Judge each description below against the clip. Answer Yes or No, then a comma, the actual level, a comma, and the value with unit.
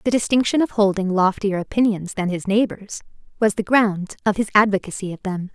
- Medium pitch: No, high, 205 Hz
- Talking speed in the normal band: Yes, average, 185 wpm